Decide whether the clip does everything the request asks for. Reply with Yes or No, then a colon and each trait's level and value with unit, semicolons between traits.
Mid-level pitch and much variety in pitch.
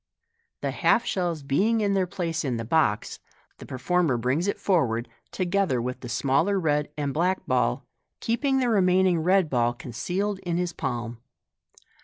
Yes: medium, 165 Hz; wide, 6.8 semitones